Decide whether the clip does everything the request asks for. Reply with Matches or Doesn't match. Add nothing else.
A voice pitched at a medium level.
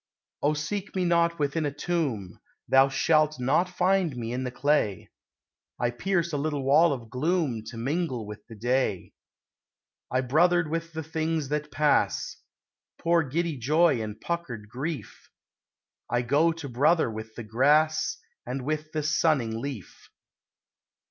Matches